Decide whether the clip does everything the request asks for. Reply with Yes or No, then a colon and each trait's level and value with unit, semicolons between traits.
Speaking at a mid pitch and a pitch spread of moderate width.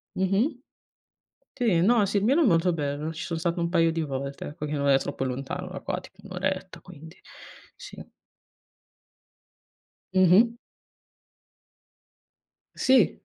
Yes: medium, 175 Hz; average, 4.0 semitones